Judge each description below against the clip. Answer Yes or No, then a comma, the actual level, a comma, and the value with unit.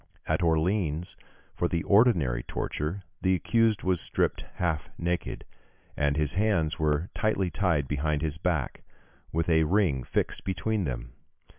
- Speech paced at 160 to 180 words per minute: No, average, 140 wpm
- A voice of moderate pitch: No, very low, 85 Hz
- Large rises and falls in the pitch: No, average, 3.7 semitones